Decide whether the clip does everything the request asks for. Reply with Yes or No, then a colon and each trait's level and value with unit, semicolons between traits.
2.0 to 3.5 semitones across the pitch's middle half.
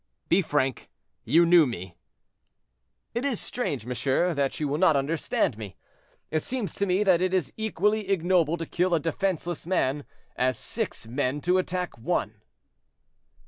No: average, 5.3 semitones